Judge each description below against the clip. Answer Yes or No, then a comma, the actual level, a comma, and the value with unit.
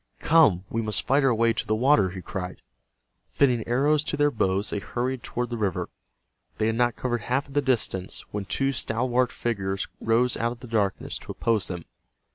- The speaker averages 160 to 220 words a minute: Yes, average, 200 wpm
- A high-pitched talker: No, low, 115 Hz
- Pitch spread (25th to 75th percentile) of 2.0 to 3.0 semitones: No, average, 3.7 semitones